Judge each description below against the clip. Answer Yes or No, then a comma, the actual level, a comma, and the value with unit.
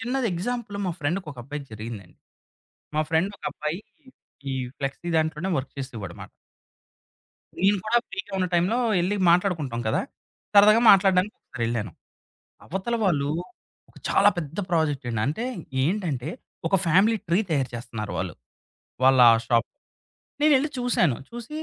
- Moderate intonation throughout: No, wide, 7.1 semitones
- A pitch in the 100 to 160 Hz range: No, medium, 170 Hz